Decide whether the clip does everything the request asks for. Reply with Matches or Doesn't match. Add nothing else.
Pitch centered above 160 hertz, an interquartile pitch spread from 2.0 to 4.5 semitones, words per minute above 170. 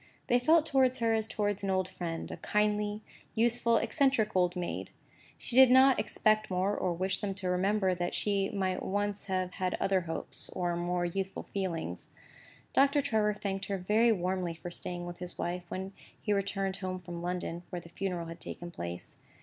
Matches